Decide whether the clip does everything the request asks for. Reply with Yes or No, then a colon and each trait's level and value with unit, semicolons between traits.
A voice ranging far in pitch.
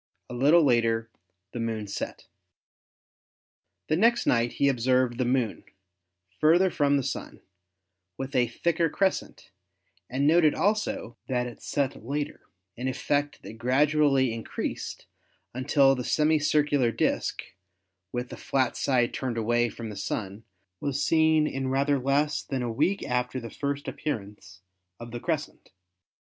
No: average, 3.8 semitones